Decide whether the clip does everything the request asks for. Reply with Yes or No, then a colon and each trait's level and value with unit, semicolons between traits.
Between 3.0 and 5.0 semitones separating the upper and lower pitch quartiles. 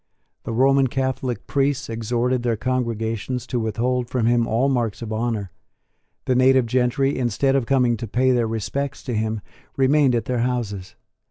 No: narrow, 2.4 semitones